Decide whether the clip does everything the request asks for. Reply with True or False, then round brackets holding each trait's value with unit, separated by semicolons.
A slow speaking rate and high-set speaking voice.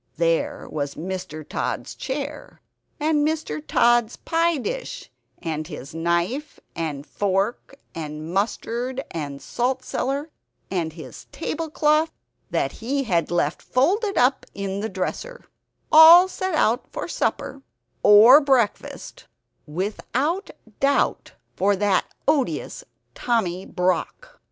True (115 wpm; 235 Hz)